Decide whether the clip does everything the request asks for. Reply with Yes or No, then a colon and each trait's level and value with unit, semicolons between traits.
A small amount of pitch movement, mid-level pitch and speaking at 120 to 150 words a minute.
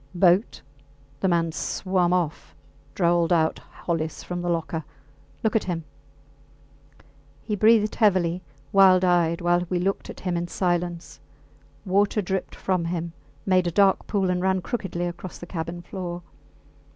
Yes: narrow, 1.7 semitones; medium, 175 Hz; average, 145 wpm